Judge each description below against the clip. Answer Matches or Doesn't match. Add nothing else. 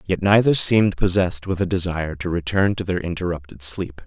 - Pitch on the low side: Matches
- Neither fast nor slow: Matches